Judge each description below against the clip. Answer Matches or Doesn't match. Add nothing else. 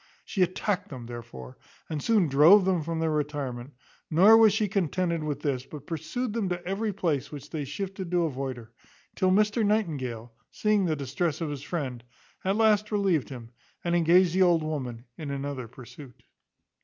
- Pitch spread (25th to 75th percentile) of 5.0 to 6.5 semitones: Matches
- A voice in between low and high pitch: Matches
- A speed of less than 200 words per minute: Matches